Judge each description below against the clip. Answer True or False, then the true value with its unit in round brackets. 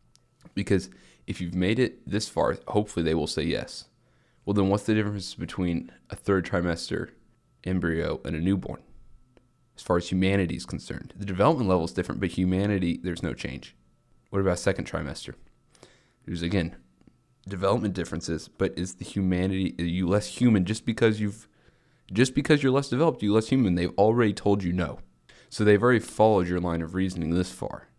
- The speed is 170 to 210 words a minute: True (180 wpm)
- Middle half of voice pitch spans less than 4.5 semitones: True (3.3 semitones)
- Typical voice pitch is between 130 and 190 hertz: False (95 Hz)